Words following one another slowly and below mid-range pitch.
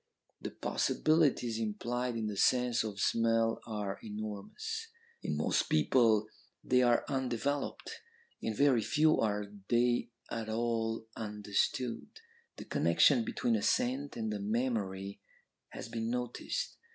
Yes: slow, 125 wpm; low, 115 Hz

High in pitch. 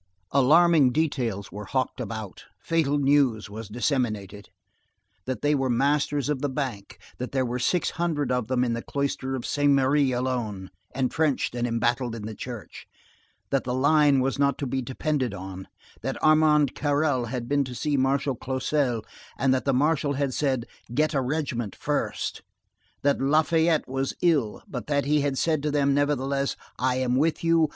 No: low, 135 Hz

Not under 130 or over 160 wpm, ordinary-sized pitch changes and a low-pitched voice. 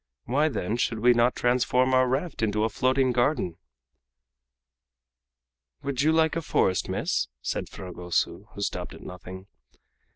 Yes: average, 140 wpm; average, 4.1 semitones; low, 125 Hz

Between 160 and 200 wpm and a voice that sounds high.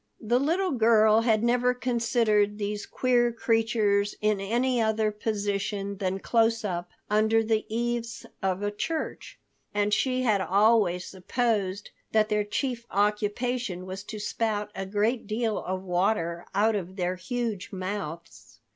No: average, 140 wpm; high, 215 Hz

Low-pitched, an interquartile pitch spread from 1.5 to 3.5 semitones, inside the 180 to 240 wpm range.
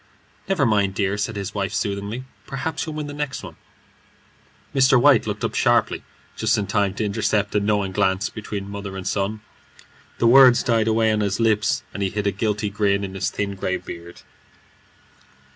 Yes: low, 105 Hz; narrow, 2.4 semitones; average, 185 wpm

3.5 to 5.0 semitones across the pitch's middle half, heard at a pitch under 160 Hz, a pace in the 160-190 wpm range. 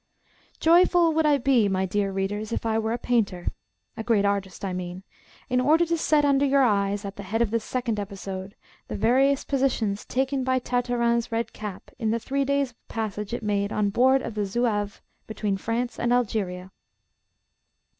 No: average, 4.4 semitones; high, 225 Hz; average, 185 wpm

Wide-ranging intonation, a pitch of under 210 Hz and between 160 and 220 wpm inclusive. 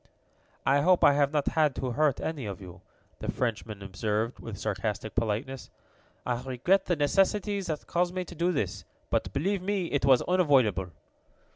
Yes: wide, 7.6 semitones; medium, 140 Hz; average, 170 wpm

